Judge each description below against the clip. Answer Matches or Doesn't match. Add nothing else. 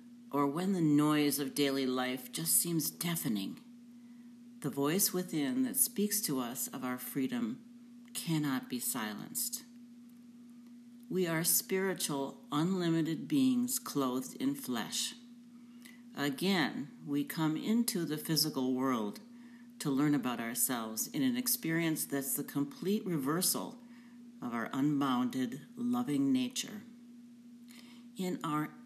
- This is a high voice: Matches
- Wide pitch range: Matches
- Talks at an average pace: Doesn't match